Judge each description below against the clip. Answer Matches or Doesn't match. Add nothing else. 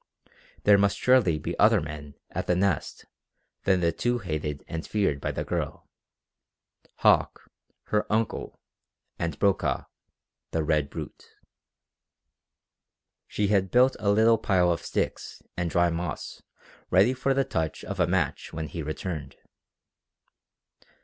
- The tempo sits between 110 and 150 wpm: Matches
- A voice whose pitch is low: Matches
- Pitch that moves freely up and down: Doesn't match